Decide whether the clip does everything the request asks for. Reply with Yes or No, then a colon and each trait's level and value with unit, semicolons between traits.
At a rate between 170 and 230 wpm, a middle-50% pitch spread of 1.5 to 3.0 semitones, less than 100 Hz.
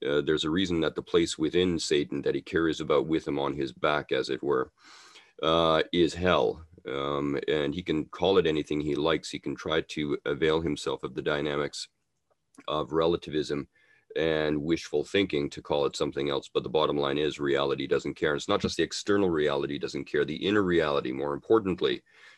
Yes: average, 200 wpm; narrow, 2.5 semitones; very low, 75 Hz